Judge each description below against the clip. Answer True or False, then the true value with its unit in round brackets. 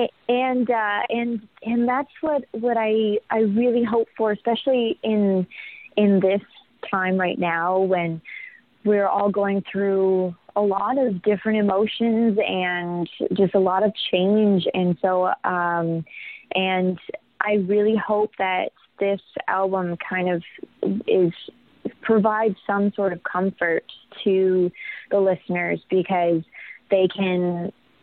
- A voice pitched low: False (200 Hz)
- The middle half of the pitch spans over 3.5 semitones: False (3.0 semitones)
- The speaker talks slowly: True (125 wpm)